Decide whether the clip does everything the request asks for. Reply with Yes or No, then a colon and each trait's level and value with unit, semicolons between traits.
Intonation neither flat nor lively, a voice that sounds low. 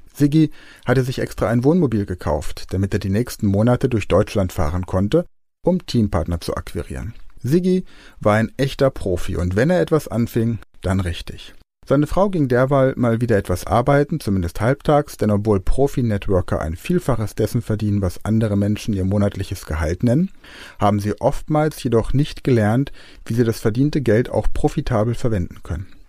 No: wide, 5.7 semitones; low, 115 Hz